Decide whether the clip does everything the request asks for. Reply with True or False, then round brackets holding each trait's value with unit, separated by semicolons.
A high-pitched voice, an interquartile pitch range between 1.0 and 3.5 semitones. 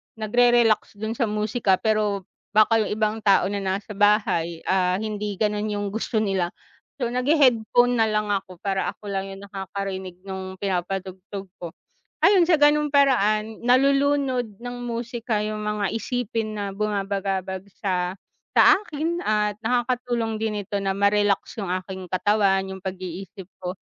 True (210 Hz; 3.1 semitones)